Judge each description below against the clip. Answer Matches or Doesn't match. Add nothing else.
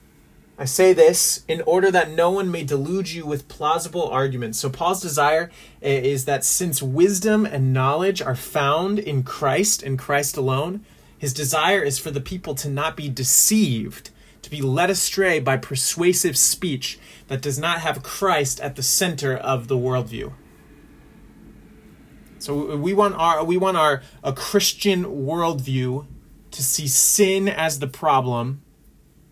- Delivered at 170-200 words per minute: Doesn't match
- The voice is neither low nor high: Matches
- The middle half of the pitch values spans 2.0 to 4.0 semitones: Doesn't match